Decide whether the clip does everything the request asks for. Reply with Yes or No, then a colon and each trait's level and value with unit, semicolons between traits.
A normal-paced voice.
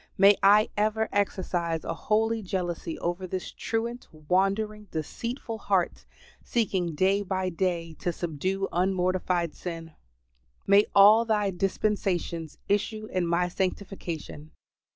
No: slow, 115 wpm